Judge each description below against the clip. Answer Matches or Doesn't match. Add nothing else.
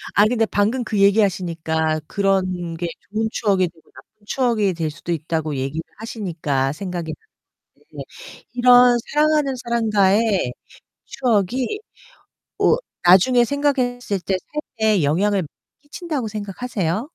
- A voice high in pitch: Matches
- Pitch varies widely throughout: Matches